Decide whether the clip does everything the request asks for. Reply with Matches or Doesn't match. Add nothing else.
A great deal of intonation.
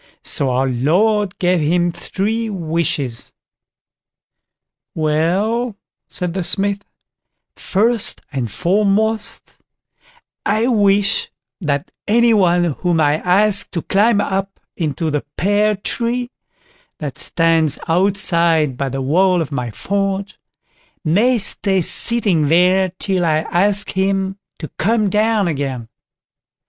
Doesn't match